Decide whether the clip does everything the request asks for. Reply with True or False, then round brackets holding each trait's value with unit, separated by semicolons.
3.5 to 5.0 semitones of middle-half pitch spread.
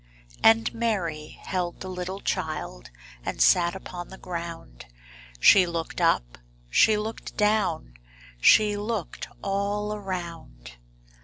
True (4.4 semitones)